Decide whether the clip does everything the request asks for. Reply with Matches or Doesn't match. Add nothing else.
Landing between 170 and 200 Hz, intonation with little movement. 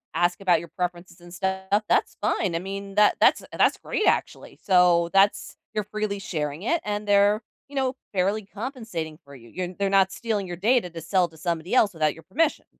Doesn't match